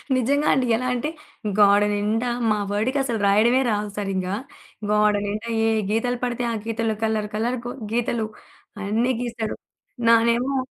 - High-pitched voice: Yes, high, 225 Hz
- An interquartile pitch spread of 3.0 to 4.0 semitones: No, narrow, 2.6 semitones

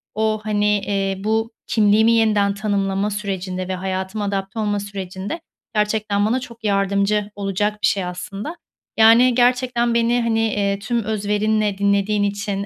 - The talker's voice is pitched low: No, high, 205 Hz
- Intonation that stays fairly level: Yes, narrow, 1.8 semitones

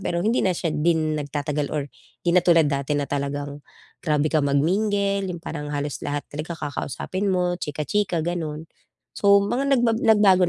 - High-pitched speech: No, medium, 160 Hz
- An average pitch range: Yes, average, 4.6 semitones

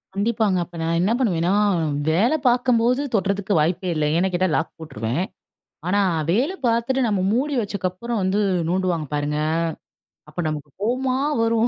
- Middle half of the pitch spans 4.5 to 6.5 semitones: Yes, wide, 5.4 semitones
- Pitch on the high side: Yes, high, 195 Hz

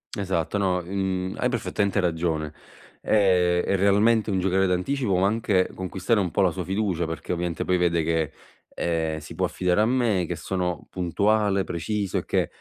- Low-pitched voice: Yes, very low, 95 Hz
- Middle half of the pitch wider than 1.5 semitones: Yes, narrow, 2.5 semitones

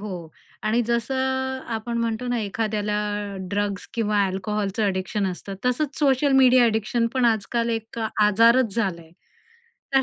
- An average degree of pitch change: Yes, average, 3.2 semitones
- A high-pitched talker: Yes, high, 225 Hz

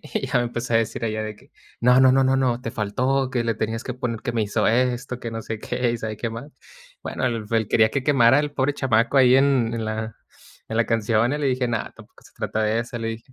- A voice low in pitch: Yes, low, 120 Hz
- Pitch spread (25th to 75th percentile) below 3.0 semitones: Yes, narrow, 2.4 semitones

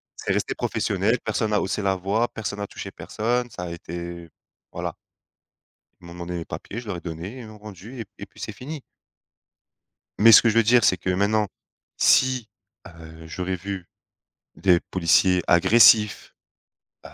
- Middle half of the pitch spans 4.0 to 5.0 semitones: Yes, average, 4.3 semitones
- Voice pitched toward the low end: Yes, low, 100 Hz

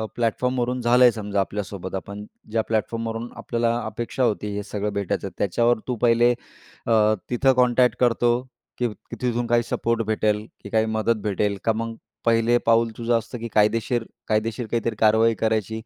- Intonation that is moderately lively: No, narrow, 1.8 semitones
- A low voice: Yes, low, 115 Hz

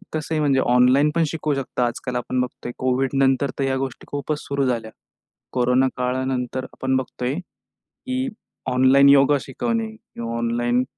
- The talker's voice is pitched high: No, low, 130 Hz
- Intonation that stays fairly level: Yes, narrow, 2.0 semitones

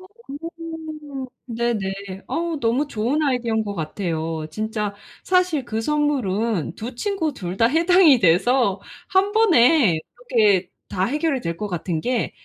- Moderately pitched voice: No, high, 245 Hz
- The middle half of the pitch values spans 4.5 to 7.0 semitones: No, wide, 7.5 semitones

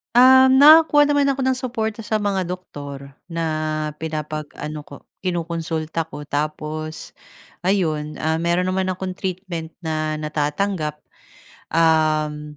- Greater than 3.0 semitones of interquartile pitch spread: Yes, average, 4.0 semitones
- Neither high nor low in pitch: Yes, medium, 165 Hz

